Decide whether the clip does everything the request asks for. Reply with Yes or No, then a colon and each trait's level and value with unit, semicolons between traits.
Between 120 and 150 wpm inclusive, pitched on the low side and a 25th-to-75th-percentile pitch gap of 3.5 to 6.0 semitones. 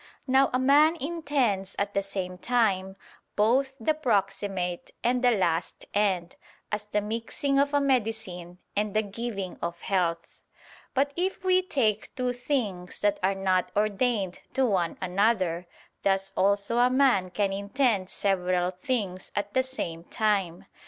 No: average, 145 wpm; high, 205 Hz; average, 5.1 semitones